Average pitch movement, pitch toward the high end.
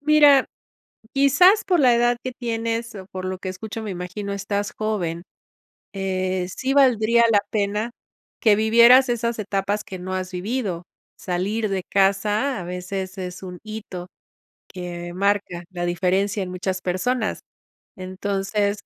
Yes: average, 3.7 semitones; high, 200 Hz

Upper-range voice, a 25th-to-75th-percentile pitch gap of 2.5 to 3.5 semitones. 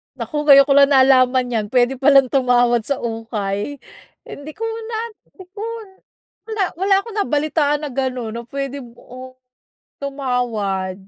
Yes: very high, 265 Hz; average, 3.1 semitones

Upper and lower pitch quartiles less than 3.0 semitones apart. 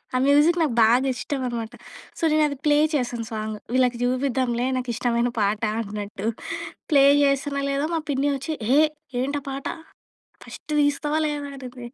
No: average, 3.3 semitones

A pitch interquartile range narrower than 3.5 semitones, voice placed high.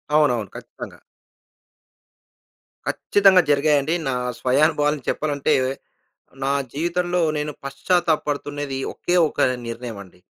No: average, 3.0 semitones; medium, 145 Hz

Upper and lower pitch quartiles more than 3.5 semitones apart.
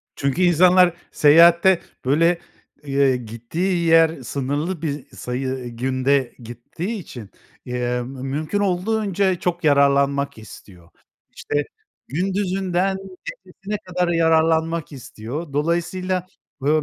Yes: average, 5.1 semitones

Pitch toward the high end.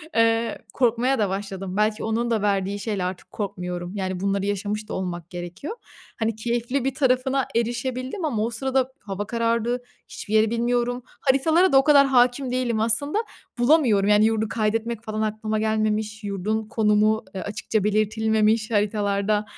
Yes: high, 220 Hz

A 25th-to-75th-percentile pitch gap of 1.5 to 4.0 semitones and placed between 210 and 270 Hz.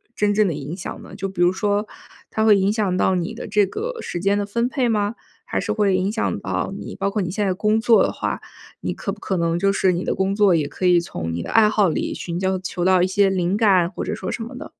No: average, 2.7 semitones; high, 195 Hz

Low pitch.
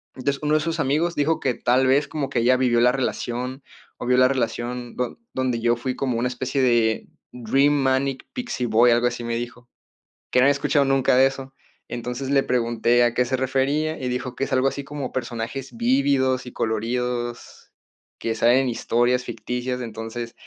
Yes: low, 125 Hz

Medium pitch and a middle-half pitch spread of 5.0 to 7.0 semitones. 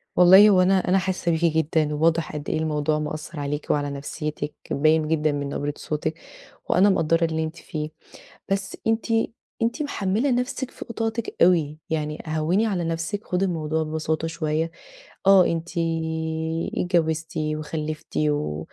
No: medium, 160 Hz; average, 3.1 semitones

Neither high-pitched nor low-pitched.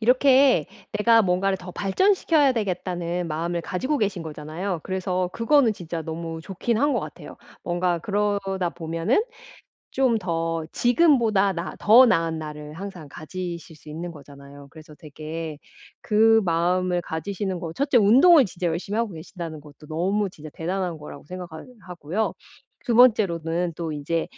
Yes: medium, 180 Hz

